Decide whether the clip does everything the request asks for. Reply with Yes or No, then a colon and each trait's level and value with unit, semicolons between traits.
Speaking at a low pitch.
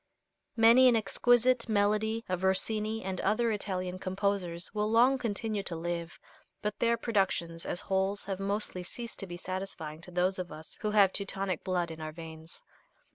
No: high, 195 Hz